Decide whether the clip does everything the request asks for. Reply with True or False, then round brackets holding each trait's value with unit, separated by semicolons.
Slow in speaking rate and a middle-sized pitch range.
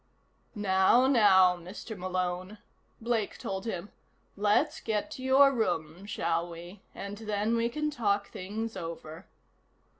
True (125 wpm; 3.7 semitones)